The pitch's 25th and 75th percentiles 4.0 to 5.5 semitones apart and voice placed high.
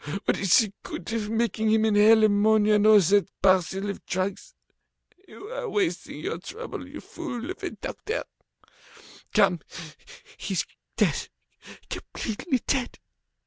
No: average, 3.3 semitones; high, 215 Hz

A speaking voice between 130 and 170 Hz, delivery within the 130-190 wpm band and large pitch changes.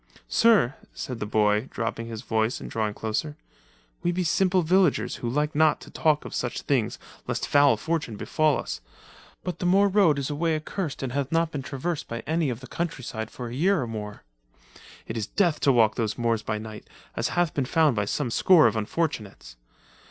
No: medium, 140 Hz; fast, 205 wpm; wide, 6.4 semitones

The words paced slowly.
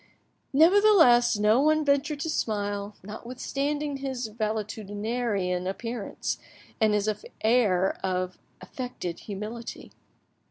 Yes: slow, 90 wpm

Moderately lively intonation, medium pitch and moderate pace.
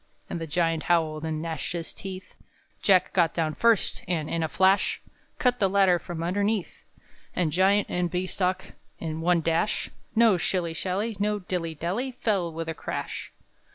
Yes: average, 3.1 semitones; medium, 180 Hz; average, 175 wpm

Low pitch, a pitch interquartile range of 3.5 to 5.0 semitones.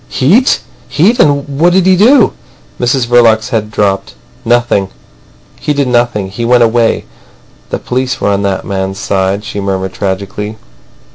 No: low, 115 Hz; wide, 5.4 semitones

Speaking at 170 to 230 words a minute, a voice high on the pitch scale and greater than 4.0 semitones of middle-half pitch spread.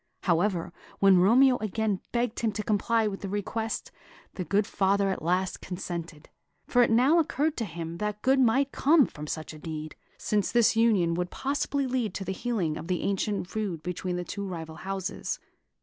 Yes: average, 185 wpm; high, 200 Hz; average, 4.5 semitones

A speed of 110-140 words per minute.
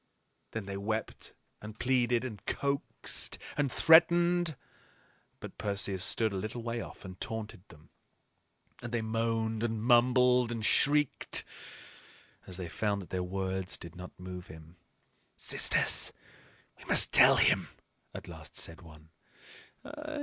Yes: slow, 135 wpm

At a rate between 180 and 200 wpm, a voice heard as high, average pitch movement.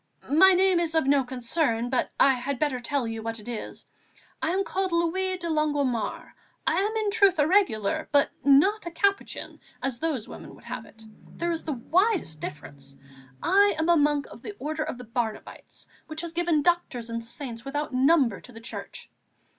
No: average, 195 wpm; very high, 295 Hz; wide, 6.0 semitones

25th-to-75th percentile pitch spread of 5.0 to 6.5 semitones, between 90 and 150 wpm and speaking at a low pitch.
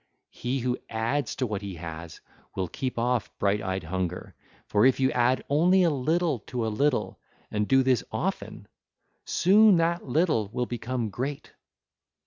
No: wide, 5.4 semitones; average, 160 wpm; low, 125 Hz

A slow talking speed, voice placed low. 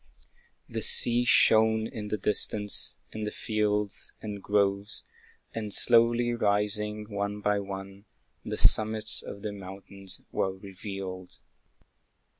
Yes: slow, 115 wpm; low, 105 Hz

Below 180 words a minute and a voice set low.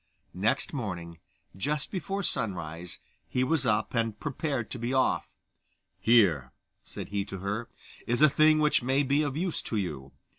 Yes: average, 160 wpm; low, 120 Hz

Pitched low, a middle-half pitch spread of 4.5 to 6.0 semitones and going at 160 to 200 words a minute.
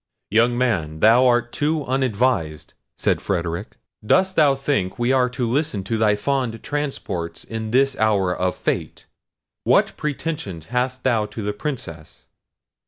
No: low, 120 Hz; average, 4.9 semitones; average, 145 wpm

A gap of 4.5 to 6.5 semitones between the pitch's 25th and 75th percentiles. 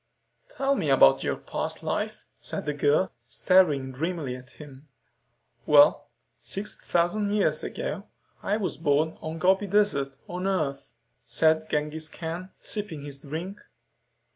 Yes: average, 4.8 semitones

